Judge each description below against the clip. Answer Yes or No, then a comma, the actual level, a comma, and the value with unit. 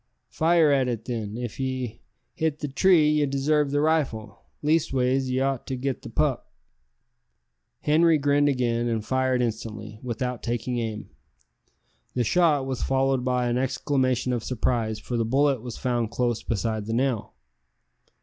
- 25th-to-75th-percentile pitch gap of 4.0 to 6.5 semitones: No, average, 3.1 semitones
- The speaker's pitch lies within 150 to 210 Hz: No, low, 130 Hz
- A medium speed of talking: Yes, average, 155 wpm